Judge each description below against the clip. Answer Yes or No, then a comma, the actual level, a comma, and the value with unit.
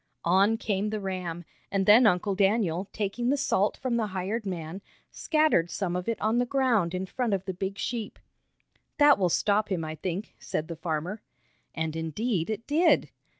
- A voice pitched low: No, high, 195 Hz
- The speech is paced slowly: No, average, 185 wpm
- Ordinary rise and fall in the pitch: Yes, average, 4.0 semitones